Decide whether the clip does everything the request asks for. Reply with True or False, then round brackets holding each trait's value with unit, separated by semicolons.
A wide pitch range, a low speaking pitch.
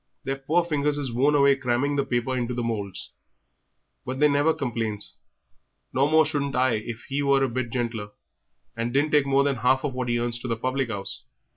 False (3.0 semitones; 130 Hz)